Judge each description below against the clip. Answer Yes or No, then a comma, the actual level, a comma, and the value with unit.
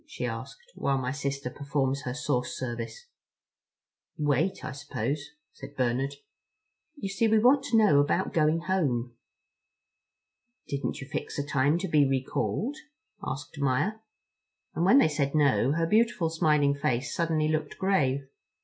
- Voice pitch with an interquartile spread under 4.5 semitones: Yes, average, 4.0 semitones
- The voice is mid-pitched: Yes, medium, 145 Hz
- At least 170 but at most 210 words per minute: No, average, 145 wpm